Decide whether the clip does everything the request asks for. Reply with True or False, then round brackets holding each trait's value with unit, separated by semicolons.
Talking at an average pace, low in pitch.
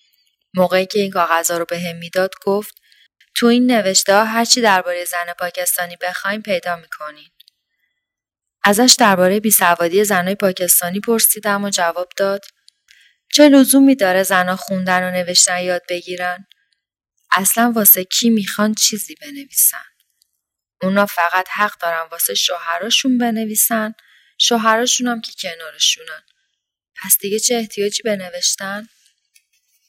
False (120 wpm; 195 Hz)